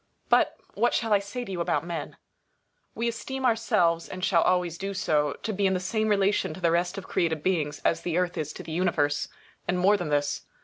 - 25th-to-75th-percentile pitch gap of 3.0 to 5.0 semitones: Yes, average, 3.6 semitones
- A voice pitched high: No, medium, 180 Hz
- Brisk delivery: Yes, fast, 225 wpm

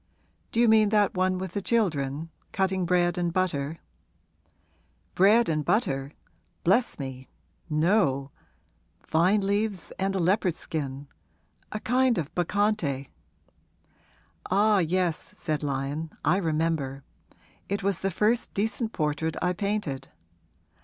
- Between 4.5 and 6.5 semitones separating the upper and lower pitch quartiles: Yes, average, 5.1 semitones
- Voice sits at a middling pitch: Yes, medium, 180 Hz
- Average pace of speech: No, slow, 120 wpm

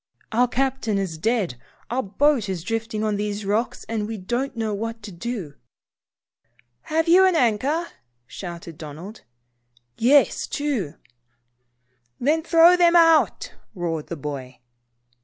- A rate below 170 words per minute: Yes, average, 140 wpm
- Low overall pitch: No, high, 220 Hz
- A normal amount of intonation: No, wide, 7.2 semitones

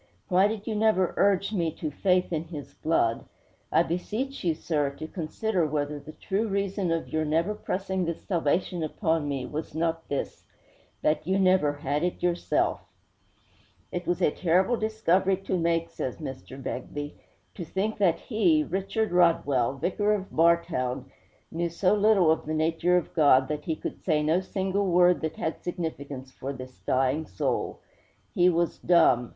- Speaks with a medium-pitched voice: Yes, medium, 170 Hz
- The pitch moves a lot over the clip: No, average, 3.9 semitones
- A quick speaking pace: No, average, 170 wpm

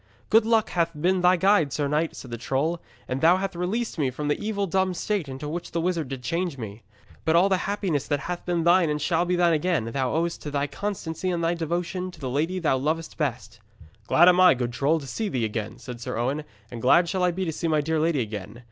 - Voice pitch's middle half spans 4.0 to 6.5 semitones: Yes, average, 4.6 semitones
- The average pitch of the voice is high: No, medium, 165 Hz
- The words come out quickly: Yes, fast, 250 wpm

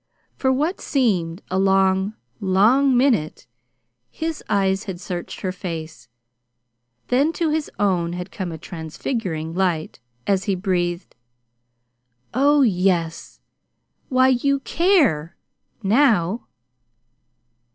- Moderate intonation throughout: No, wide, 6.8 semitones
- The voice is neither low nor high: No, high, 195 Hz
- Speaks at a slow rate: Yes, slow, 105 wpm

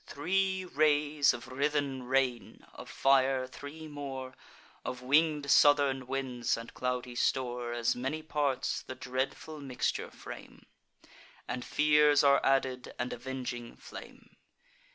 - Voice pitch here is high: No, low, 135 Hz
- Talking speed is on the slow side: Yes, slow, 120 wpm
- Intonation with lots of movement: No, narrow, 2.5 semitones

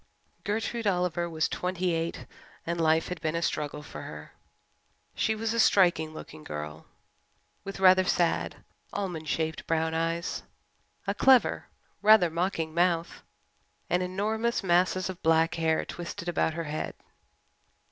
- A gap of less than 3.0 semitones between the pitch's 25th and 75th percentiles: Yes, narrow, 2.6 semitones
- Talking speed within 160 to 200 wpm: No, slow, 135 wpm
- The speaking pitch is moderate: Yes, medium, 170 Hz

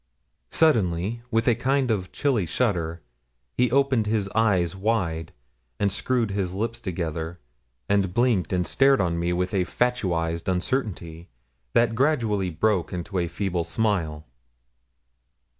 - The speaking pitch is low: Yes, low, 100 Hz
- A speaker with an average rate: No, slow, 130 wpm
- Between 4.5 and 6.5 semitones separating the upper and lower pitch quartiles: Yes, average, 5.0 semitones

